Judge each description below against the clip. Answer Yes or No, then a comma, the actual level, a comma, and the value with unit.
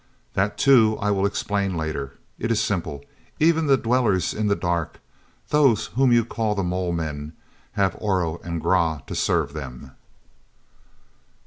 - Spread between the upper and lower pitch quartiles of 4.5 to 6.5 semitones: Yes, average, 5.2 semitones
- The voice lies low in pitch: Yes, very low, 95 Hz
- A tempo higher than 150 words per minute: No, average, 140 wpm